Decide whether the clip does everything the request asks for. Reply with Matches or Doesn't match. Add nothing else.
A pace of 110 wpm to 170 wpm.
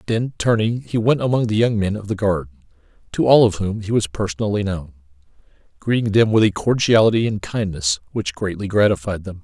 Doesn't match